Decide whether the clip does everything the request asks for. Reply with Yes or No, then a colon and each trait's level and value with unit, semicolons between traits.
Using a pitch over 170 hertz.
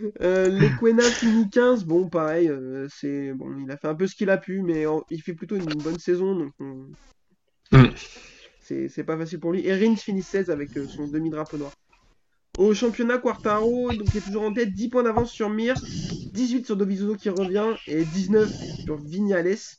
Yes: high, 190 Hz